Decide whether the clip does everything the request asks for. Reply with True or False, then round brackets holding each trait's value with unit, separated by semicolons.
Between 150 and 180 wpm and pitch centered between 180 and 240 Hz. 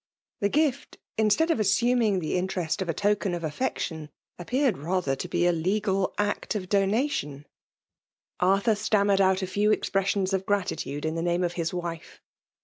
True (165 wpm; 190 Hz)